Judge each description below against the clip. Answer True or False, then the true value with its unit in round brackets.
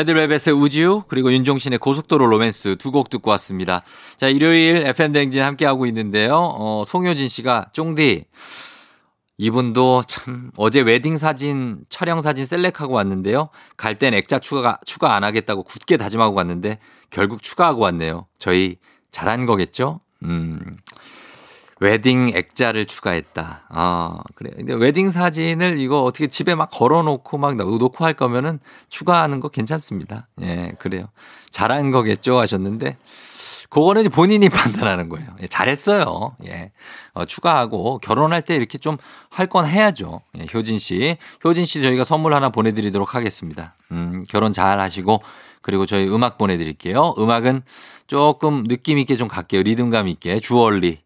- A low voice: True (125 Hz)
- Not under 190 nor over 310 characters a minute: False (325 characters per minute)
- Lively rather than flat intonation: True (6.4 semitones)